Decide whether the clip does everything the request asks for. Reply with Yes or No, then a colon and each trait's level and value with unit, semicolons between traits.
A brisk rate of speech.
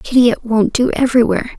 No: average, 190 wpm